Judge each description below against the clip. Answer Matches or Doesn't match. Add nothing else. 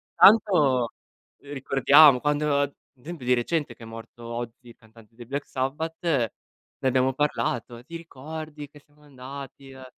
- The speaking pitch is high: Doesn't match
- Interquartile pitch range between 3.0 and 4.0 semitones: Matches